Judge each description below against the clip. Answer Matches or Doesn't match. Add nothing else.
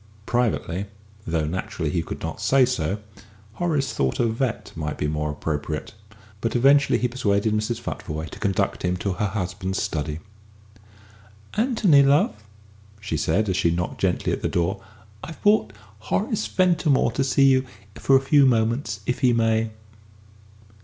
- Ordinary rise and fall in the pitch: Doesn't match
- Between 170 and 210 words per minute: Doesn't match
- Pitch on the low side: Matches